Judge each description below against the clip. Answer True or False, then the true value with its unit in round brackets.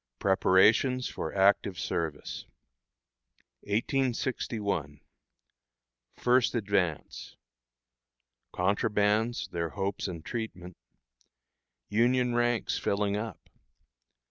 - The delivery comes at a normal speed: False (65 wpm)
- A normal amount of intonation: True (4.2 semitones)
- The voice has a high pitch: False (105 Hz)